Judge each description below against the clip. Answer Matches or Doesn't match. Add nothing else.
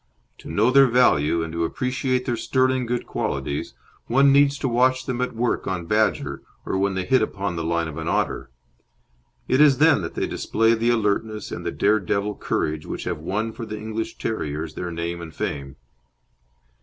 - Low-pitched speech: Matches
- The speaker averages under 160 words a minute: Doesn't match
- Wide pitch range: Matches